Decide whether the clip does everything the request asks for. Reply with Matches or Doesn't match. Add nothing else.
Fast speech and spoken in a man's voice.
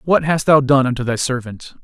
Matches